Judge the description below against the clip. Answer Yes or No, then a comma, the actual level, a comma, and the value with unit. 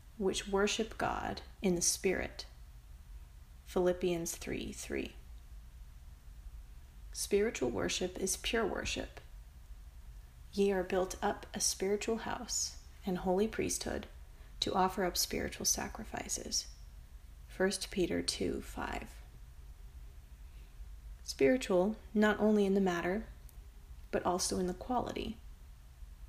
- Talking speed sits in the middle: No, slow, 100 wpm